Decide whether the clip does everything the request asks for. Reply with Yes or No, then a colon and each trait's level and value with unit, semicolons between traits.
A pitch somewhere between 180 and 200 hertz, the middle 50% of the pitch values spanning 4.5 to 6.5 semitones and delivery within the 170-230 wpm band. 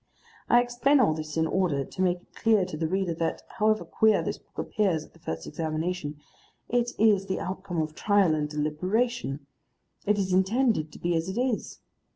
Yes: medium, 185 Hz; wide, 5.4 semitones; average, 190 wpm